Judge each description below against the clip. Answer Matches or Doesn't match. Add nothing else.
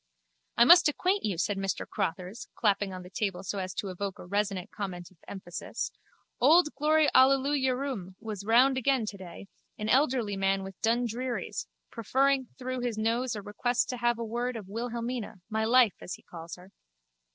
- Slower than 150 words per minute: Doesn't match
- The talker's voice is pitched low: Doesn't match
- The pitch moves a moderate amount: Matches